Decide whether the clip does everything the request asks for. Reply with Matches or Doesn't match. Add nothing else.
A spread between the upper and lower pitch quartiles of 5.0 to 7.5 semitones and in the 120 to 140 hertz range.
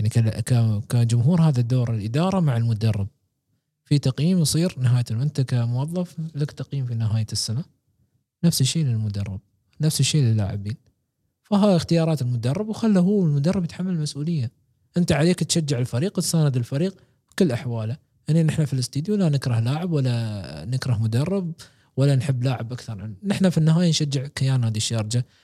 Matches